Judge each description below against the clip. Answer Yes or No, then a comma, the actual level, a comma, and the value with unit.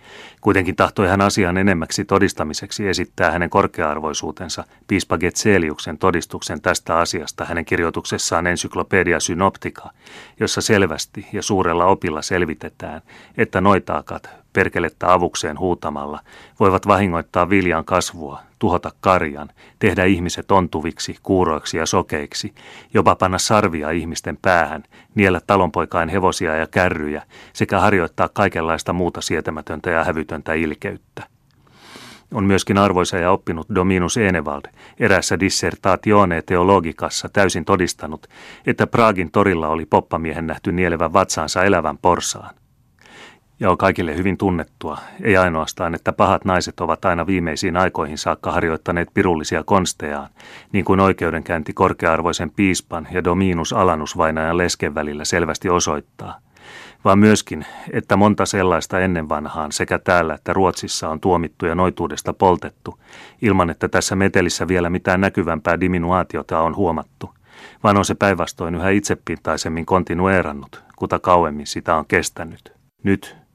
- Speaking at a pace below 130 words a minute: Yes, average, 120 wpm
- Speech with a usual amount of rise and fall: Yes, average, 3.1 semitones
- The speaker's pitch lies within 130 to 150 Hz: No, very low, 90 Hz